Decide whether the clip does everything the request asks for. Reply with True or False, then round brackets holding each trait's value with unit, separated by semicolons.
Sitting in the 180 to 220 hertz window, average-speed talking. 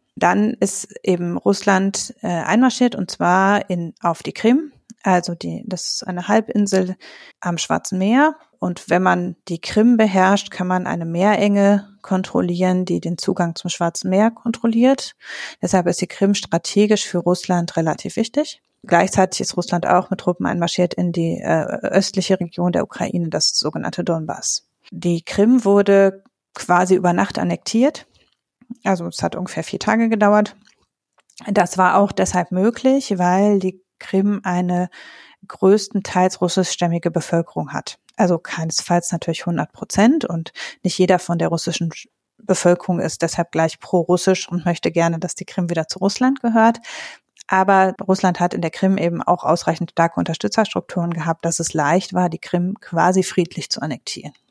True (185 Hz; 150 wpm)